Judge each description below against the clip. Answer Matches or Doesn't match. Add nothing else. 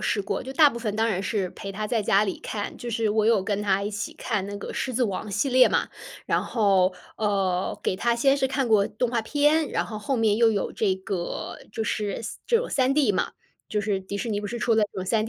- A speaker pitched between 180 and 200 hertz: Doesn't match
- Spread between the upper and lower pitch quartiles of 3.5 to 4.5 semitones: Doesn't match